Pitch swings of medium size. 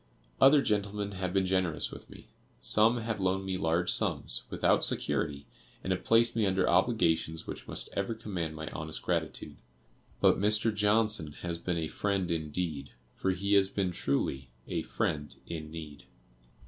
Yes: average, 4.3 semitones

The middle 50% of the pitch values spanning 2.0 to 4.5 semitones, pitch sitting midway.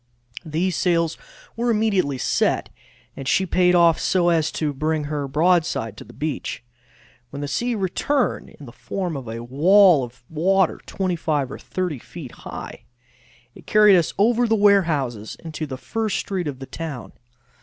No: average, 5.2 semitones; medium, 165 Hz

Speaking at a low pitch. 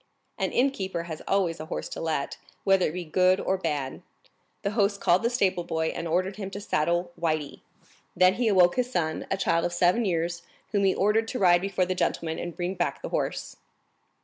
No: medium, 180 Hz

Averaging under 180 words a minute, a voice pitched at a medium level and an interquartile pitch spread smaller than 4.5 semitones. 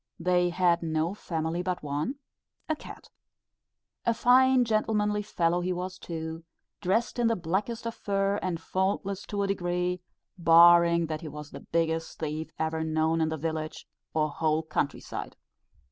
Yes: average, 160 wpm; medium, 175 Hz; average, 3.6 semitones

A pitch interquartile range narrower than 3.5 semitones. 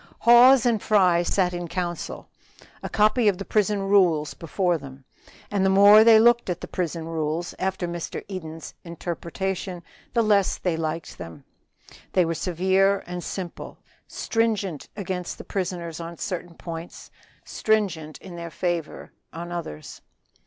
Yes: average, 3.0 semitones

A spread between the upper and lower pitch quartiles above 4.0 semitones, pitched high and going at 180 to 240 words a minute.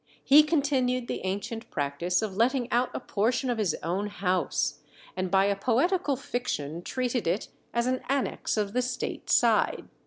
No: average, 5.0 semitones; high, 235 Hz; average, 165 wpm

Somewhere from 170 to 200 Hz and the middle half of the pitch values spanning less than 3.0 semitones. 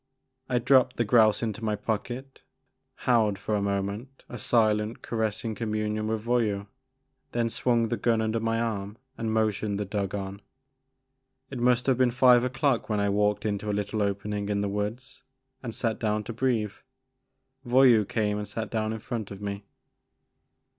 No: low, 110 Hz; narrow, 2.4 semitones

